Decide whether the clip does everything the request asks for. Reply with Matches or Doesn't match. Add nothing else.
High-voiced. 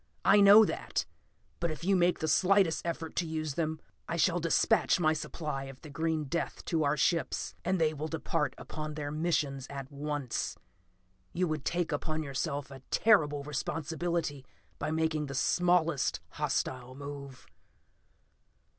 Doesn't match